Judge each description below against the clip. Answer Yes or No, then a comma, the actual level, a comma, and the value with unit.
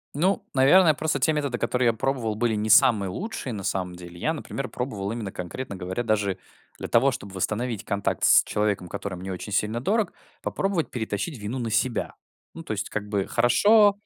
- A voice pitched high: No, low, 115 Hz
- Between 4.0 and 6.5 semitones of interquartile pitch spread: Yes, average, 5.3 semitones